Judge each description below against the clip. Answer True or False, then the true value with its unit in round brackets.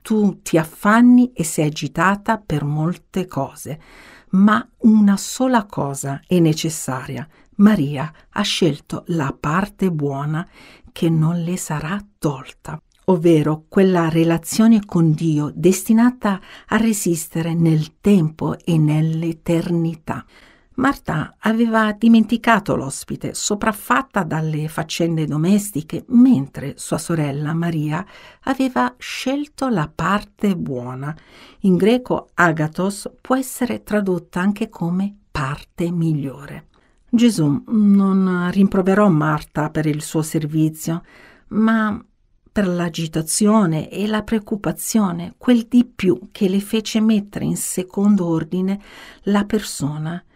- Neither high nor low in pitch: True (180 Hz)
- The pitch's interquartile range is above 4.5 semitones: True (5.2 semitones)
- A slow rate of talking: True (110 wpm)